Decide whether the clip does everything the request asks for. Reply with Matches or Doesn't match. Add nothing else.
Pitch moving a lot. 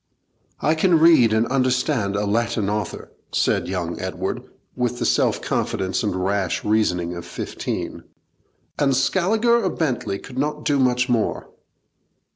Matches